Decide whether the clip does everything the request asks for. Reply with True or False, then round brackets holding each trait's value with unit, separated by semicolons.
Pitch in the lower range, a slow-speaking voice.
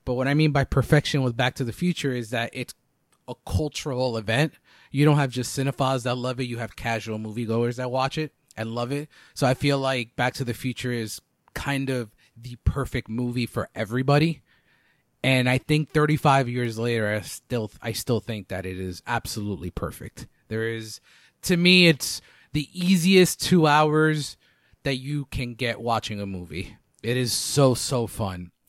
False (125 Hz; 185 wpm)